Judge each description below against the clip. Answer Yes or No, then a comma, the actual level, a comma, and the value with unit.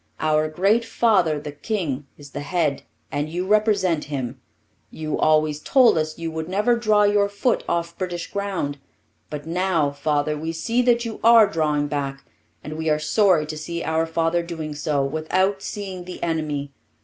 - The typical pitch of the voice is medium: Yes, medium, 165 Hz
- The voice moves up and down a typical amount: Yes, average, 4.4 semitones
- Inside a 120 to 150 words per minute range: No, average, 175 wpm